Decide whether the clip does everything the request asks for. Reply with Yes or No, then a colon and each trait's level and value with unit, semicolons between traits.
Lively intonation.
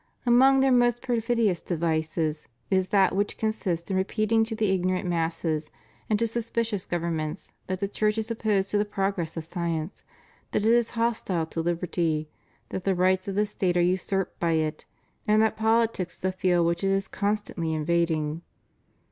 No: average, 4.3 semitones